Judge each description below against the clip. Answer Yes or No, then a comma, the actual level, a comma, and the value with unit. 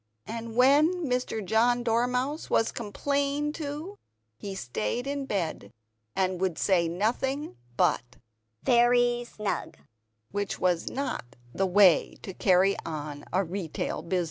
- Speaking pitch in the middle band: No, high, 220 Hz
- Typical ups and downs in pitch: No, wide, 6.0 semitones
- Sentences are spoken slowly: Yes, slow, 125 wpm